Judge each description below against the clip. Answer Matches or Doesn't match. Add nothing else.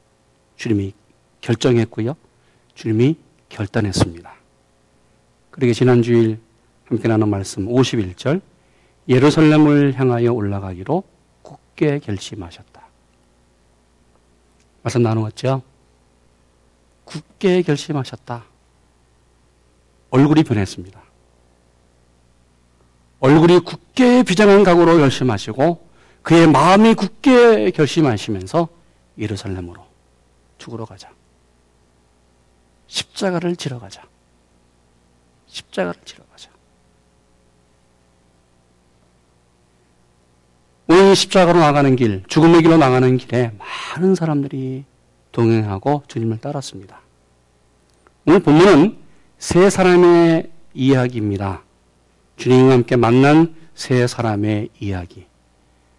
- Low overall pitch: Matches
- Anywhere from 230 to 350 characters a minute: Doesn't match